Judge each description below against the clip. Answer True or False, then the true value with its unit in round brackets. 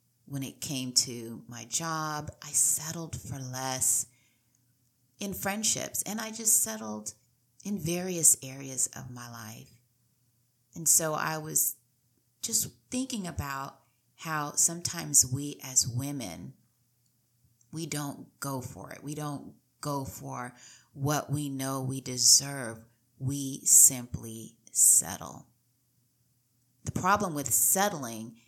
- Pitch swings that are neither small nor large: True (3.2 semitones)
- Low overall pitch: True (130 Hz)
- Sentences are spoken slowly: True (115 wpm)